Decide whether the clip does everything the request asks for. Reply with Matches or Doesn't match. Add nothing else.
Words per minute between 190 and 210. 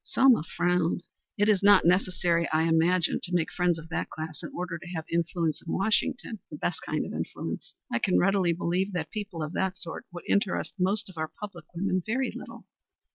Matches